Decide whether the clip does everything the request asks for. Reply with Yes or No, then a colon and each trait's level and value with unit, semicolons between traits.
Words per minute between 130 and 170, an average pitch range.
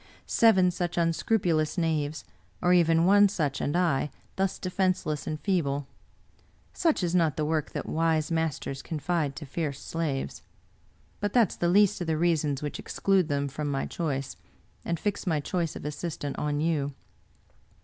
Yes: average, 160 wpm; average, 3.3 semitones